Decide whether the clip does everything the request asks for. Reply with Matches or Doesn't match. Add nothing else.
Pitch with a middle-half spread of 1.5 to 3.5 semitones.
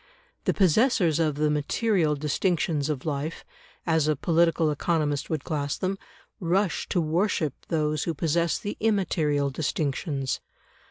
Matches